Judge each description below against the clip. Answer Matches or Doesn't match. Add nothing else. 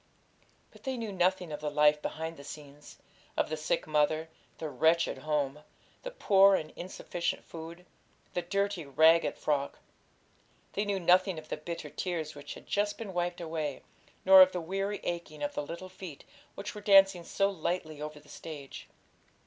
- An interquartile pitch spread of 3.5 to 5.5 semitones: Matches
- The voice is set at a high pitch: Doesn't match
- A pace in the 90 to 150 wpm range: Doesn't match